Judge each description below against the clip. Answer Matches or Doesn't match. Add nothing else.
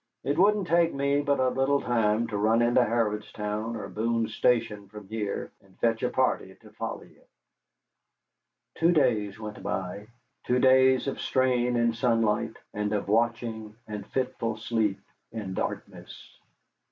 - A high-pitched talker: Doesn't match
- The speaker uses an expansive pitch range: Doesn't match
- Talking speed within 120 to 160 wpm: Matches